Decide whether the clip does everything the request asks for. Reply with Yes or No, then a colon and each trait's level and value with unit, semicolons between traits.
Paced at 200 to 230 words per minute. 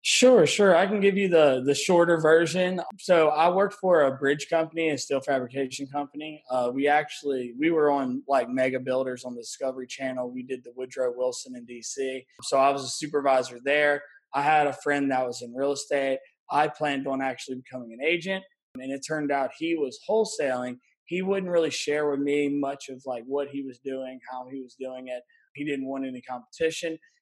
Yes: fast, 205 wpm